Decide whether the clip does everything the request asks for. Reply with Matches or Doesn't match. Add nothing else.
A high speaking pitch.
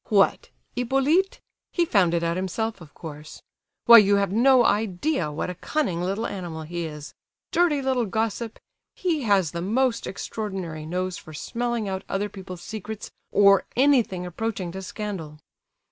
Matches